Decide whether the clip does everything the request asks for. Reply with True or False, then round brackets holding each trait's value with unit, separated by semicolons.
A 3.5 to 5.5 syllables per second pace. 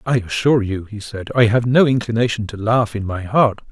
True (5.4 syllables/s)